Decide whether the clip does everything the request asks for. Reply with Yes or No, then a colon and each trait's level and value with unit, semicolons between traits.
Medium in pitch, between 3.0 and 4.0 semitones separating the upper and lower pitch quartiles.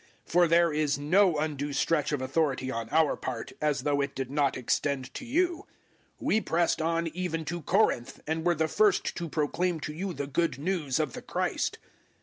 Yes: medium, 155 Hz; average, 3.4 semitones